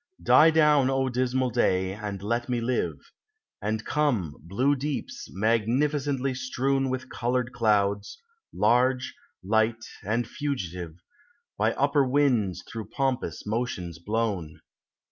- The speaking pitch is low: Yes, low, 120 Hz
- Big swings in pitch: No, average, 4.3 semitones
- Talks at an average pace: No, slow, 125 wpm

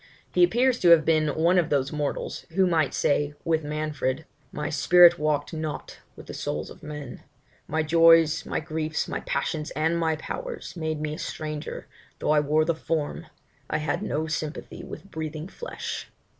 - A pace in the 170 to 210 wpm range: Yes, average, 175 wpm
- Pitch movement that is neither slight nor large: No, narrow, 1.7 semitones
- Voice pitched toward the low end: No, medium, 155 Hz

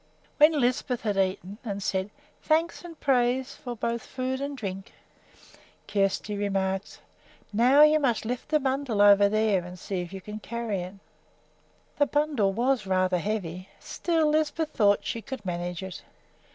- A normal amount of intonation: No, wide, 5.7 semitones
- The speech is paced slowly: No, average, 160 wpm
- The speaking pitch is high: Yes, high, 220 Hz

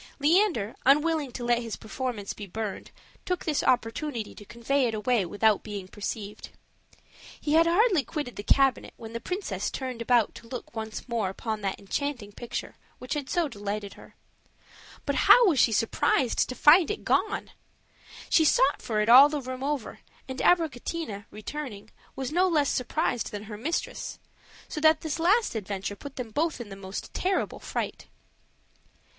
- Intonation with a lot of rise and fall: Yes, wide, 5.9 semitones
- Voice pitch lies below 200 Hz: No, high, 245 Hz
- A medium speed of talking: Yes, average, 170 wpm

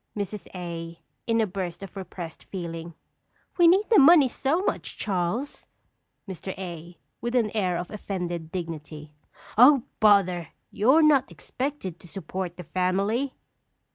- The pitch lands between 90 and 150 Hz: No, high, 190 Hz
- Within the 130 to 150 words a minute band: Yes, average, 140 wpm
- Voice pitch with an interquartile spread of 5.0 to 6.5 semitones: Yes, wide, 5.6 semitones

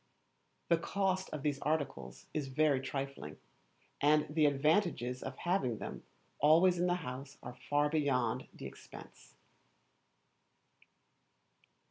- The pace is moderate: No, slow, 115 wpm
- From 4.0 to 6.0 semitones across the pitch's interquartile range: No, average, 3.6 semitones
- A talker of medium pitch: Yes, medium, 145 Hz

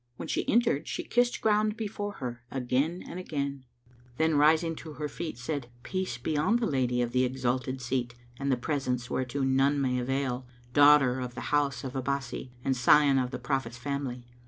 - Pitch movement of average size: Yes, average, 3.2 semitones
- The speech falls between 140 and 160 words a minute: No, average, 180 wpm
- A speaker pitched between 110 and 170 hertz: Yes, low, 135 Hz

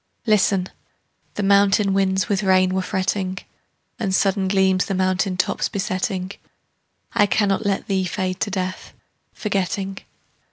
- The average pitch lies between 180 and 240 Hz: Yes, high, 190 Hz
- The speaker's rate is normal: No, slow, 130 wpm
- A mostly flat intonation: Yes, narrow, 1.2 semitones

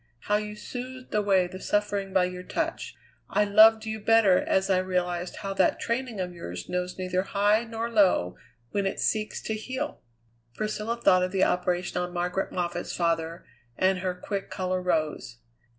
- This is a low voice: No, high, 190 Hz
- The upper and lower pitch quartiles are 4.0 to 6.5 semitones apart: No, average, 2.9 semitones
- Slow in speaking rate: No, average, 170 wpm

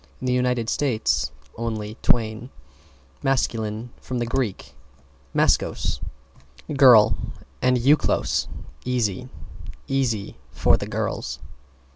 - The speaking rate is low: Yes, slow, 90 wpm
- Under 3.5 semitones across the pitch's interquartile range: Yes, average, 2.7 semitones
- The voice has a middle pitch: No, low, 120 Hz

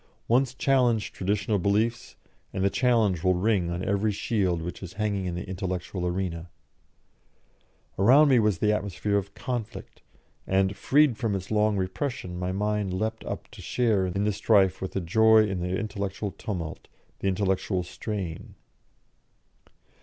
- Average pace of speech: Yes, average, 155 wpm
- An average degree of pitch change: Yes, average, 3.0 semitones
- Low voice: Yes, low, 100 Hz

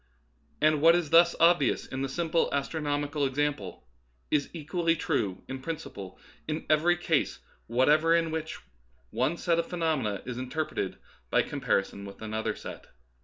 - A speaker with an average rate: Yes, average, 155 wpm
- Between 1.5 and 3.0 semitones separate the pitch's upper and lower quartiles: No, average, 4.0 semitones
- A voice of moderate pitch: Yes, medium, 150 Hz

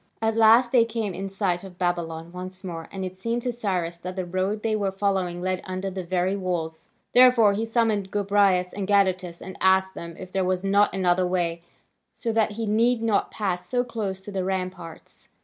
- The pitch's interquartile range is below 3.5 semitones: Yes, average, 2.7 semitones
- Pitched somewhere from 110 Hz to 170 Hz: No, high, 190 Hz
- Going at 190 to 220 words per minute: Yes, average, 200 wpm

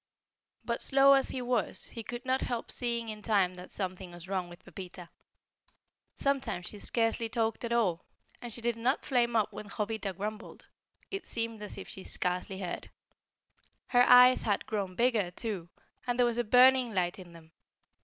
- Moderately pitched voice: No, high, 220 Hz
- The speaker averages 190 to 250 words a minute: No, average, 180 wpm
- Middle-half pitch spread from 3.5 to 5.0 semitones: Yes, average, 4.3 semitones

